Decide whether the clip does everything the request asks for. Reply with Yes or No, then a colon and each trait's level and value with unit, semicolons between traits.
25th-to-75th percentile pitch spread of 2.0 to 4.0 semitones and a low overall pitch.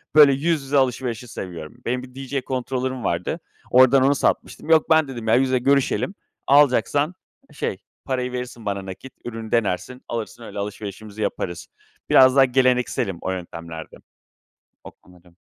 No: average, 4.5 semitones; low, 125 Hz